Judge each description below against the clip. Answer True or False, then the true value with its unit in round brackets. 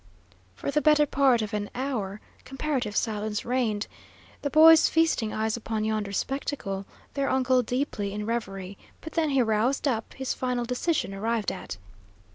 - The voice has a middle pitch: False (235 Hz)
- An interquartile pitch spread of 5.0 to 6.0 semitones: False (4.5 semitones)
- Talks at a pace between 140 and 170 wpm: True (155 wpm)